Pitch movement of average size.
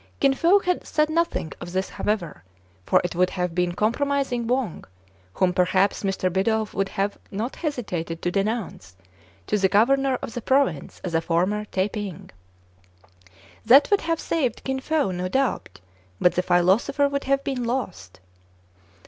No: wide, 6.9 semitones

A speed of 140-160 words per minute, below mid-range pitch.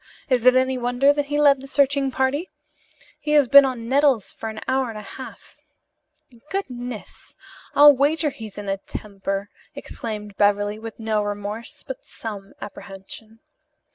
No: average, 155 wpm; high, 245 Hz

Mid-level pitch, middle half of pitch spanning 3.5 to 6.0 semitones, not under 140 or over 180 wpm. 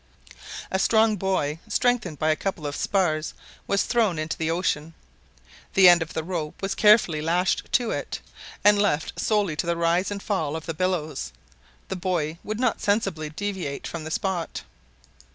Yes: medium, 175 Hz; average, 4.2 semitones; average, 170 wpm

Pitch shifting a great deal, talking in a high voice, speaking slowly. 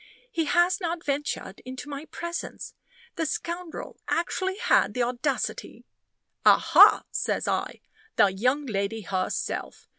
Yes: wide, 6.0 semitones; very high, 290 Hz; slow, 125 wpm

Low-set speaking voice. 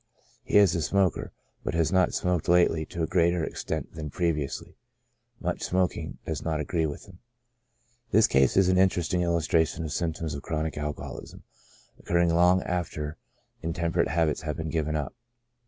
Yes: very low, 85 Hz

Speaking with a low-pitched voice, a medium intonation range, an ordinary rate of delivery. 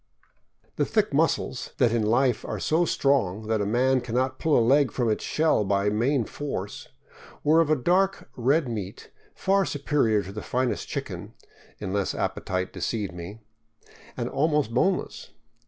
No: low, 125 Hz; wide, 5.7 semitones; average, 170 wpm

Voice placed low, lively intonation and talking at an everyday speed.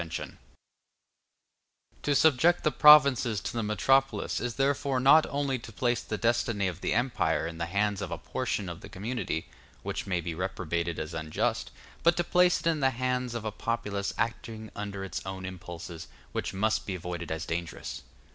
Yes: low, 110 Hz; wide, 6.3 semitones; average, 180 wpm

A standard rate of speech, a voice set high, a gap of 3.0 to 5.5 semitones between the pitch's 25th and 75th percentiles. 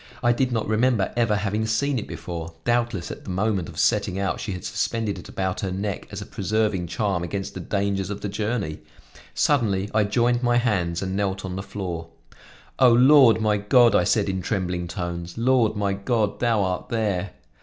No: average, 195 wpm; low, 105 Hz; average, 3.4 semitones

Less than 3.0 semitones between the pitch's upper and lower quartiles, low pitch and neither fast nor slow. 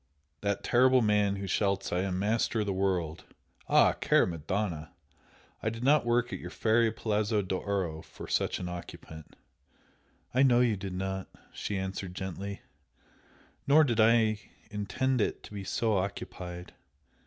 No: average, 3.3 semitones; low, 100 Hz; average, 155 wpm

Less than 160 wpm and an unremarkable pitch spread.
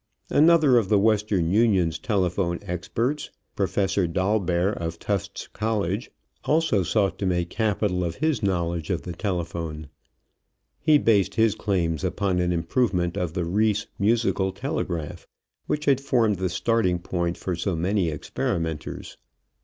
Yes: average, 140 wpm; average, 4.0 semitones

